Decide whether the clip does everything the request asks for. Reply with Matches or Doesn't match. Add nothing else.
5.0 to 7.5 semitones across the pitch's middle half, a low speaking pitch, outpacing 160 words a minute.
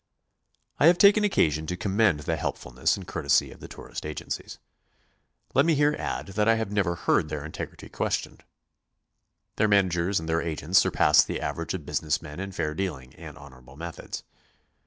Matches